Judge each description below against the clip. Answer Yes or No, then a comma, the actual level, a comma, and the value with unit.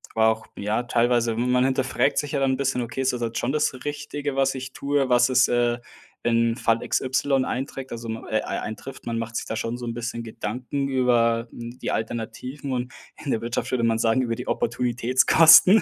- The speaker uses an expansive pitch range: No, narrow, 2.4 semitones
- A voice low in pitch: Yes, low, 125 Hz